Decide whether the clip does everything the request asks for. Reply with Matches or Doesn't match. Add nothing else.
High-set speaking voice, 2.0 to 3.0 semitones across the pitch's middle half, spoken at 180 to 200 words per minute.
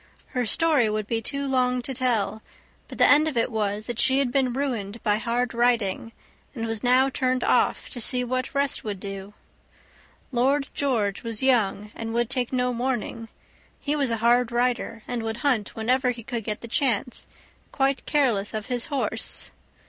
Matches